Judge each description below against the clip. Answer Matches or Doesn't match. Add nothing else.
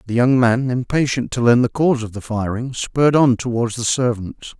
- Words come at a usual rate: Doesn't match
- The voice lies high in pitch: Doesn't match